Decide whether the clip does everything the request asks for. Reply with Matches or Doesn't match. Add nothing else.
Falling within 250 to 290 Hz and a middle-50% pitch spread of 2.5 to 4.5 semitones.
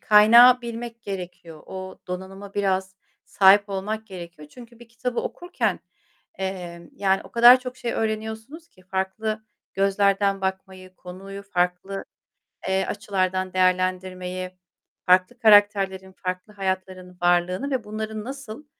Doesn't match